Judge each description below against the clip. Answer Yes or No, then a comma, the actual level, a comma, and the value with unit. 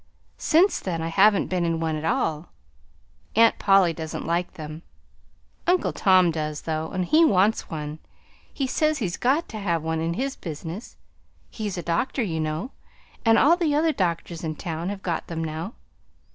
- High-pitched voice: No, medium, 175 Hz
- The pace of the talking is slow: No, average, 175 wpm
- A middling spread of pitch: No, wide, 5.7 semitones